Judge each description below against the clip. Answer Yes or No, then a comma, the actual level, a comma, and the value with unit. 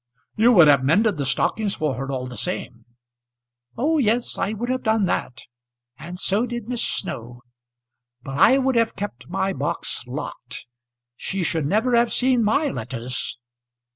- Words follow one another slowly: No, average, 165 wpm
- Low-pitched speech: No, high, 195 Hz